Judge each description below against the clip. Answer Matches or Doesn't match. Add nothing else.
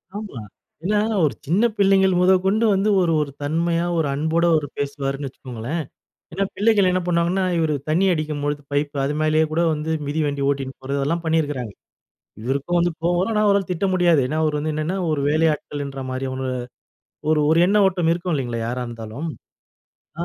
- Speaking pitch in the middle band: Matches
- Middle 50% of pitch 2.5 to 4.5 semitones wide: Matches